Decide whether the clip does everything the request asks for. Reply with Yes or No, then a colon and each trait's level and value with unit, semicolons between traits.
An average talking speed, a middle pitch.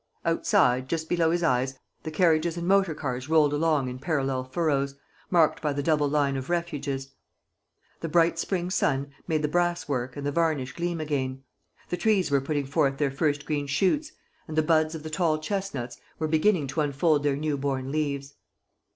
Yes: average, 185 wpm; medium, 150 Hz